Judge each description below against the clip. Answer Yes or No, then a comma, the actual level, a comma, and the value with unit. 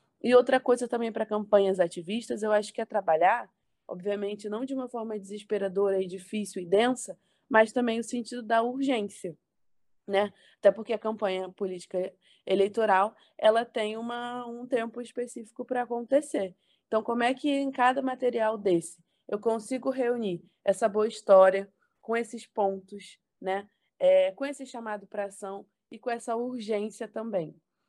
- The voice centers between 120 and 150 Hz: No, high, 220 Hz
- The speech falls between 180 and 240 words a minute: No, average, 155 wpm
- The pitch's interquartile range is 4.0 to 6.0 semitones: No, average, 3.5 semitones